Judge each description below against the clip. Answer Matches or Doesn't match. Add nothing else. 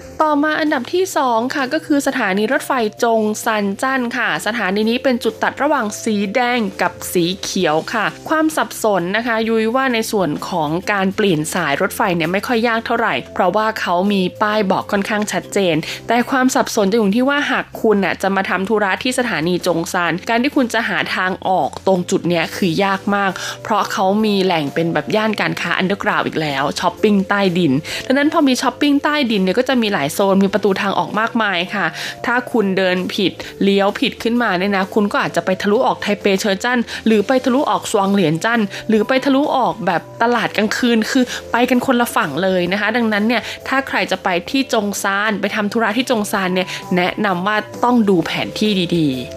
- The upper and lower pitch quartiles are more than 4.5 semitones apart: Doesn't match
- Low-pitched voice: Doesn't match